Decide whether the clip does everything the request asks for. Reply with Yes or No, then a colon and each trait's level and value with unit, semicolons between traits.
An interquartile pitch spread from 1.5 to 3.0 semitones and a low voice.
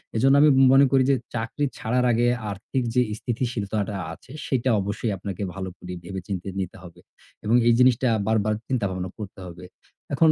No: average, 4.7 semitones; low, 110 Hz